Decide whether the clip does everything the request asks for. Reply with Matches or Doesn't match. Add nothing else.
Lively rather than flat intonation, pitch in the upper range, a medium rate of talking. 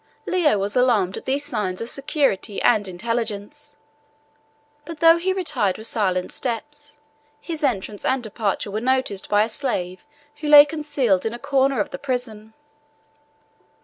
Matches